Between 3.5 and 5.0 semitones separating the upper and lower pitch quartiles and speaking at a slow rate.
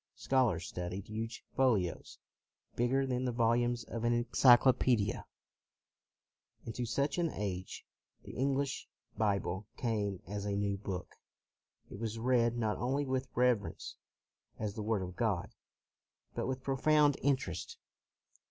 Yes: average, 4.0 semitones; slow, 130 wpm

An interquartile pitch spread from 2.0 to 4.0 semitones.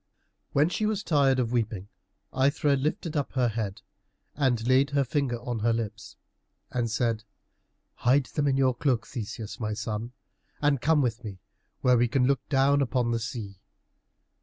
Yes: average, 3.5 semitones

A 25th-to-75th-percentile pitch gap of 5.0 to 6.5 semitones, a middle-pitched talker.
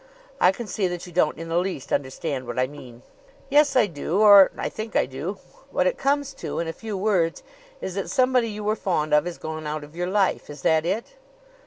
Yes: wide, 5.6 semitones; medium, 180 Hz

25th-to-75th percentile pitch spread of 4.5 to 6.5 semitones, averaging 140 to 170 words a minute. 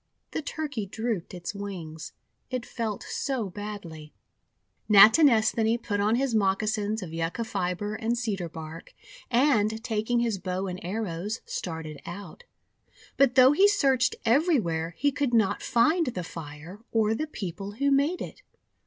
Yes: average, 5.2 semitones; average, 145 wpm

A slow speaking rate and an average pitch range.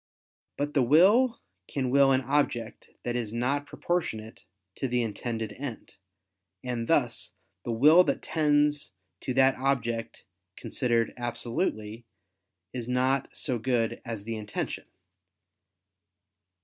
Yes: slow, 120 wpm; average, 3.5 semitones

